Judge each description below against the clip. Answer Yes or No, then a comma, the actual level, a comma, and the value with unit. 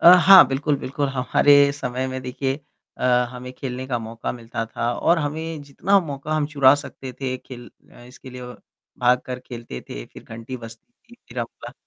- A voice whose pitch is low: Yes, low, 130 Hz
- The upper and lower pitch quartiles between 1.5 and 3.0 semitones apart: Yes, narrow, 2.6 semitones